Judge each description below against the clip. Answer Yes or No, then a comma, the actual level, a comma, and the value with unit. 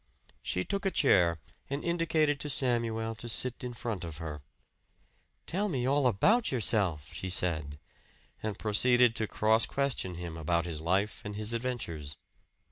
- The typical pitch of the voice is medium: No, low, 110 Hz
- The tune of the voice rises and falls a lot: Yes, wide, 6.5 semitones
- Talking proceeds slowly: No, average, 155 wpm